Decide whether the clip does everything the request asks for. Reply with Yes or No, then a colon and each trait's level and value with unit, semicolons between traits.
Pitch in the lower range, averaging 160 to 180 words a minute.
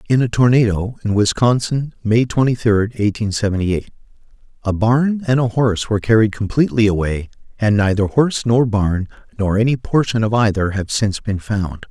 Yes: low, 110 Hz; average, 170 wpm